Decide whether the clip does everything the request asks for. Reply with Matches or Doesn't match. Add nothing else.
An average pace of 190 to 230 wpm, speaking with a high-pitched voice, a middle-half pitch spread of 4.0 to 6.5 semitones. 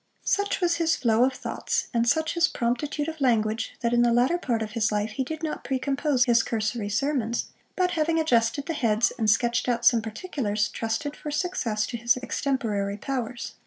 Matches